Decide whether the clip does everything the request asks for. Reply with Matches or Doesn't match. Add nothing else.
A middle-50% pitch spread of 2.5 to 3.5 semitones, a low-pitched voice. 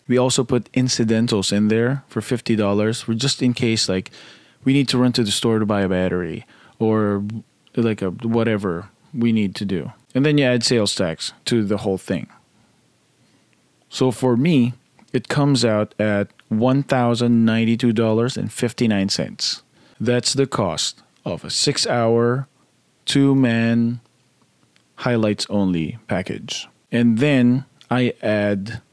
Matches